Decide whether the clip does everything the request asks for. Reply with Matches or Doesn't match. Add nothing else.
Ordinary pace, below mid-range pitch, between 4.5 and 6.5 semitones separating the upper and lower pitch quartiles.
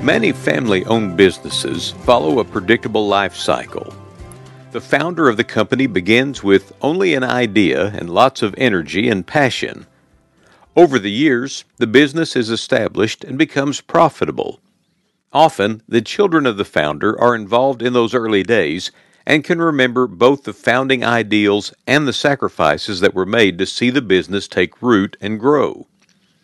Matches